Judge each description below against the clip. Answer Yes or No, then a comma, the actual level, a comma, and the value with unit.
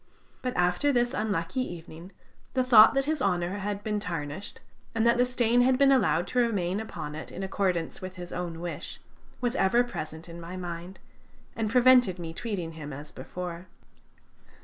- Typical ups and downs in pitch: No, wide, 5.8 semitones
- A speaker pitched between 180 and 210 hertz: Yes, high, 190 Hz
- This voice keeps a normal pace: Yes, average, 175 wpm